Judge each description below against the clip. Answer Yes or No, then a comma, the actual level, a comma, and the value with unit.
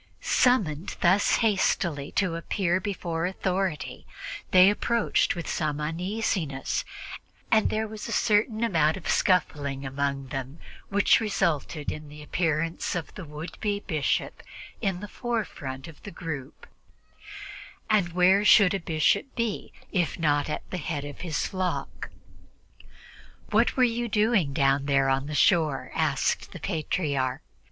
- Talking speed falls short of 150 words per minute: Yes, average, 140 wpm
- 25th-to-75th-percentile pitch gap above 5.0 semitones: Yes, wide, 5.5 semitones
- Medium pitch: Yes, medium, 170 Hz